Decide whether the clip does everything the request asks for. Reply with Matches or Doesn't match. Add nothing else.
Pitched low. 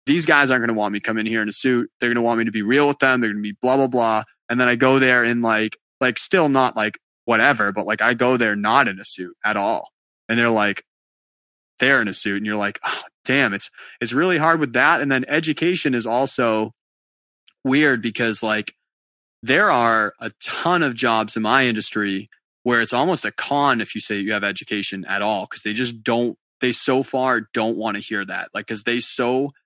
Matches